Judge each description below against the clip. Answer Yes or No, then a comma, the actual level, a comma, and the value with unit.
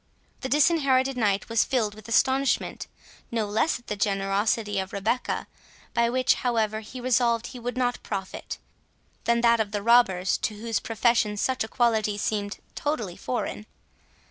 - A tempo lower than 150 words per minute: No, average, 155 wpm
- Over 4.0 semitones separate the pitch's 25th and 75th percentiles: No, average, 3.0 semitones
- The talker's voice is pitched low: No, high, 230 Hz